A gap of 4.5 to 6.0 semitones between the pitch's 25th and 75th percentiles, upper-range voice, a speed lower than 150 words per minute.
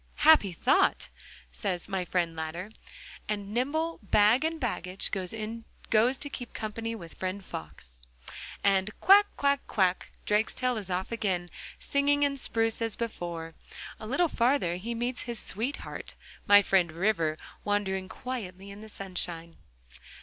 Yes: average, 4.8 semitones; high, 210 Hz; slow, 135 wpm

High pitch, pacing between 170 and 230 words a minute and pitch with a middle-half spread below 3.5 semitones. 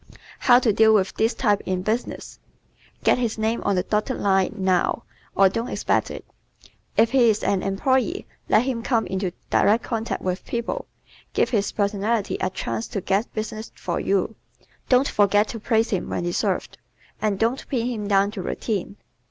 Yes: high, 215 Hz; average, 180 wpm; average, 3.0 semitones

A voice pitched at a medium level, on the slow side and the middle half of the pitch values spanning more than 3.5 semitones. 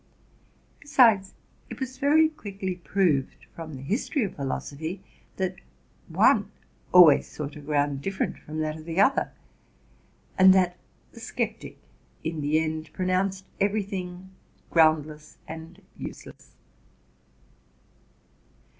Yes: medium, 180 Hz; slow, 115 wpm; average, 3.9 semitones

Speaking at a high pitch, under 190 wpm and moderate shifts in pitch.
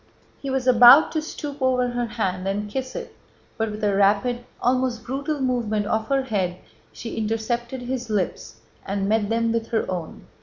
Yes: high, 230 Hz; average, 180 wpm; average, 3.5 semitones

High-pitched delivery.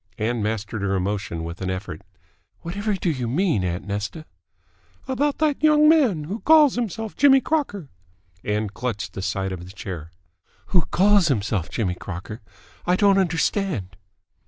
No: low, 125 Hz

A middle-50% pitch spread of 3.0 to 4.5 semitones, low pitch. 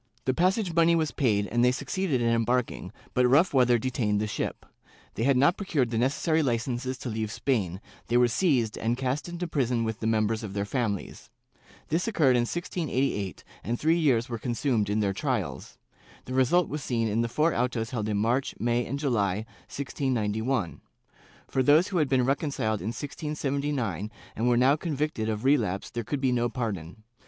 Yes: average, 4.2 semitones; low, 125 Hz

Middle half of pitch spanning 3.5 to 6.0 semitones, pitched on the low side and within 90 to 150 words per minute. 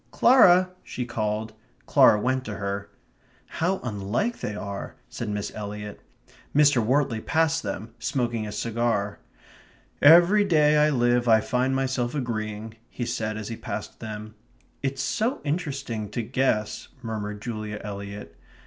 Yes: average, 4.6 semitones; low, 115 Hz; average, 145 wpm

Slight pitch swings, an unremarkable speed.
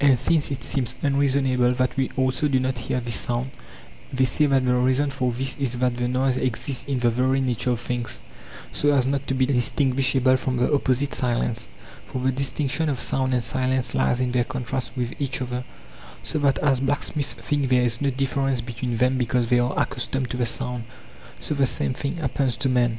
No: narrow, 1.6 semitones; fast, 210 wpm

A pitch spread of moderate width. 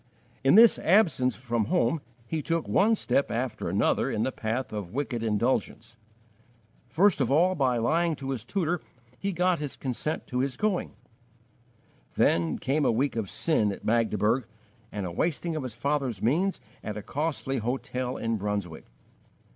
No: wide, 6.0 semitones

